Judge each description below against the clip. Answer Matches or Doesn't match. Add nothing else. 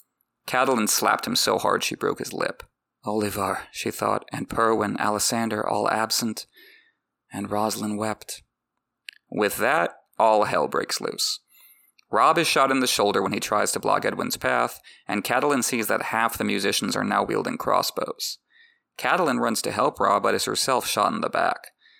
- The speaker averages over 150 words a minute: Matches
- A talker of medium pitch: Doesn't match